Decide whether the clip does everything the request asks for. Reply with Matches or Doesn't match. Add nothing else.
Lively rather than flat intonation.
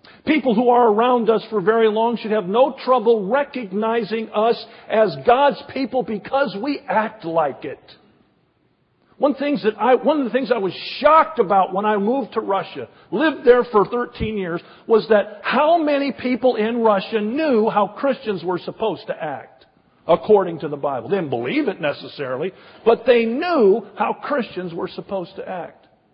Doesn't match